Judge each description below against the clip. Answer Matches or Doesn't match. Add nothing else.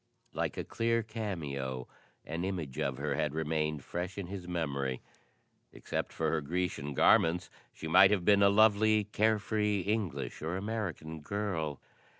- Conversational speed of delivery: Matches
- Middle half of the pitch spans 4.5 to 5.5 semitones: Matches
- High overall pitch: Doesn't match